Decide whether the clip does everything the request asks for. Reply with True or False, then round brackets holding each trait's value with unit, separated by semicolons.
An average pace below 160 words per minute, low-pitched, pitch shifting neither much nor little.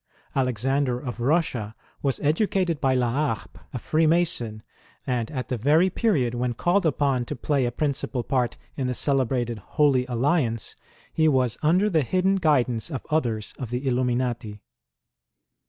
True (150 wpm; 130 Hz; 4.1 semitones)